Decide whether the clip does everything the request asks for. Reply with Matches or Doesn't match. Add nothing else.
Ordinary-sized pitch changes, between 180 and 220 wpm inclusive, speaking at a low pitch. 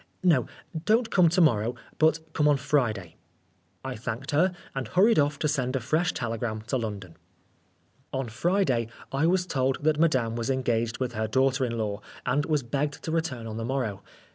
Matches